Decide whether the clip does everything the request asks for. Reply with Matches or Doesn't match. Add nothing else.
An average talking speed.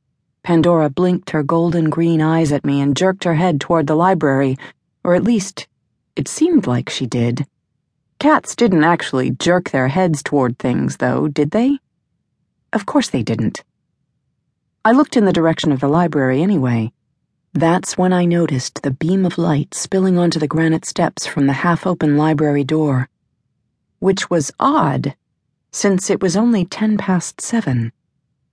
Matches